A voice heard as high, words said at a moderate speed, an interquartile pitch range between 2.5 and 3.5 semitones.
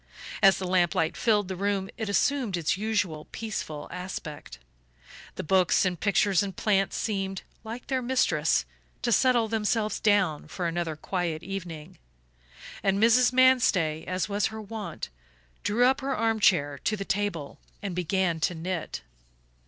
No: high, 195 Hz; average, 150 wpm; average, 4.1 semitones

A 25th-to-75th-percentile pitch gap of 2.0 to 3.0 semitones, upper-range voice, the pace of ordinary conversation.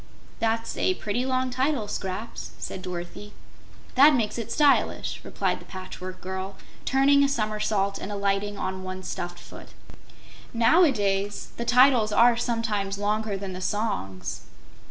No: average, 3.9 semitones; high, 210 Hz; average, 150 wpm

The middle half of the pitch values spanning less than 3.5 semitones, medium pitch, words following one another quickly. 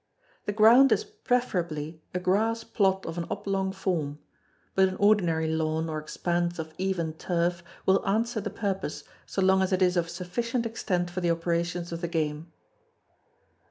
No: average, 3.1 semitones; medium, 180 Hz; average, 165 wpm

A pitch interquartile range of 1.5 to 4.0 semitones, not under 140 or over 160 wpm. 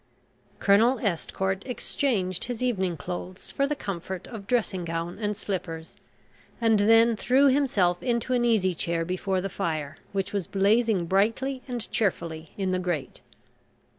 No: average, 4.6 semitones; average, 145 wpm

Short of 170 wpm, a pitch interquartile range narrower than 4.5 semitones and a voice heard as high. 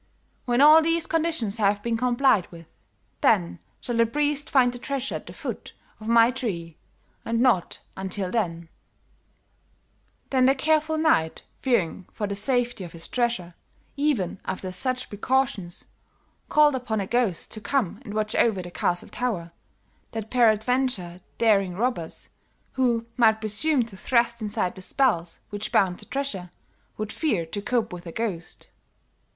No: average, 155 wpm; average, 5.3 semitones; high, 225 Hz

